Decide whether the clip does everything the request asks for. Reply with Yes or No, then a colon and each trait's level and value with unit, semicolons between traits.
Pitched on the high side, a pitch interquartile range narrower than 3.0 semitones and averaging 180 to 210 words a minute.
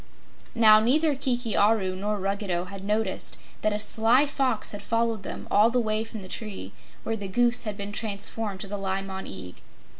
Yes: high, 210 Hz; narrow, 2.6 semitones; average, 190 wpm